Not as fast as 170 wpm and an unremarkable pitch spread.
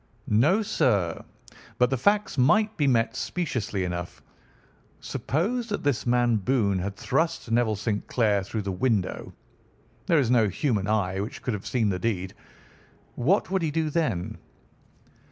No: average, 155 wpm; wide, 7.2 semitones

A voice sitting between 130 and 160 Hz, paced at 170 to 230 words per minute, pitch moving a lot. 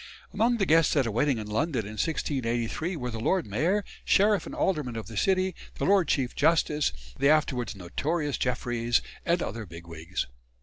Yes: medium, 140 Hz; average, 175 wpm; wide, 6.8 semitones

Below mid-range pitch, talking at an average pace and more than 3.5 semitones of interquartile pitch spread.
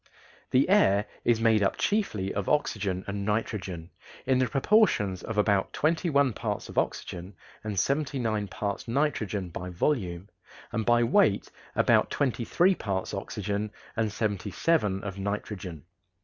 Yes: low, 105 Hz; average, 150 wpm; average, 4.9 semitones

